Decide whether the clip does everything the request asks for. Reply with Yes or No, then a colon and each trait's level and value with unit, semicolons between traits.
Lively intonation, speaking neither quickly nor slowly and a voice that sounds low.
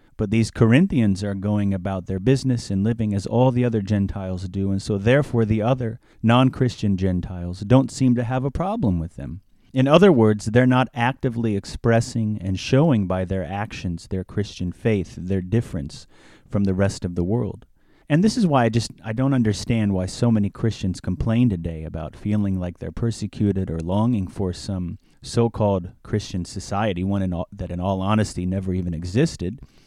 No: average, 3.8 semitones; average, 185 wpm; low, 105 Hz